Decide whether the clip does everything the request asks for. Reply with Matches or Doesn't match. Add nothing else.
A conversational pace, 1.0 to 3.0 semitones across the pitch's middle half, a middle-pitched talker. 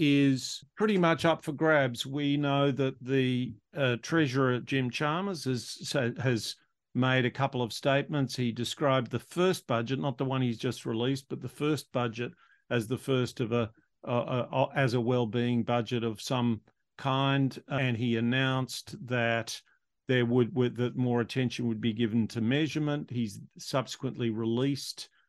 Doesn't match